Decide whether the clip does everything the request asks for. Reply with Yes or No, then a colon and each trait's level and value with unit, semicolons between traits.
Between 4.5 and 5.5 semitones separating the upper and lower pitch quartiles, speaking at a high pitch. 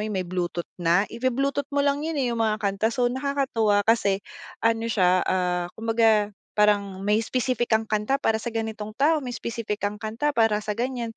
No: average, 3.1 semitones; high, 220 Hz